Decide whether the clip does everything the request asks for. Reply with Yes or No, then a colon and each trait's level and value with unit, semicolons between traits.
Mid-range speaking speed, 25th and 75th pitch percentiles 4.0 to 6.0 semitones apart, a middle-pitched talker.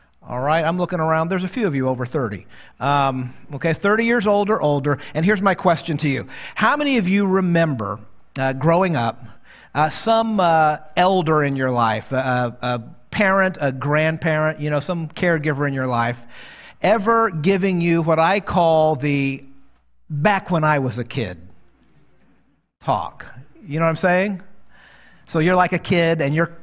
Yes: average, 175 wpm; wide, 5.4 semitones; medium, 155 Hz